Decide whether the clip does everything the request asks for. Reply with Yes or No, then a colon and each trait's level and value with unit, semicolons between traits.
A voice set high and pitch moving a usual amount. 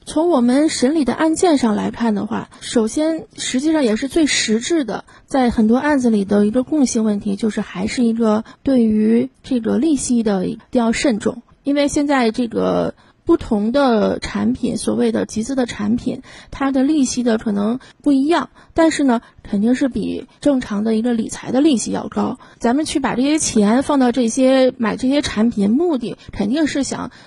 Yes: high, 245 Hz; average, 4.1 semitones